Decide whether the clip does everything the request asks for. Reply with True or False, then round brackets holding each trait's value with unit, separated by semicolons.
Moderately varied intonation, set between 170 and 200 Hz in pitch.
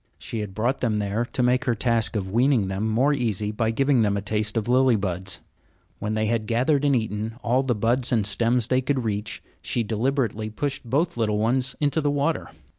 False (3.4 semitones; 115 Hz)